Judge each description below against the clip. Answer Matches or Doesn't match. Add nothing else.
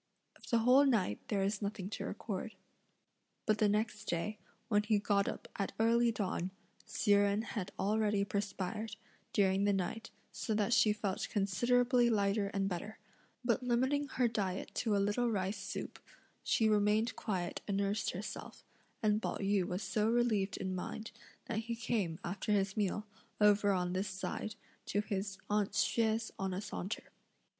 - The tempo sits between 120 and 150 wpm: Doesn't match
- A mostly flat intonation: Matches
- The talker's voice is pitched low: Doesn't match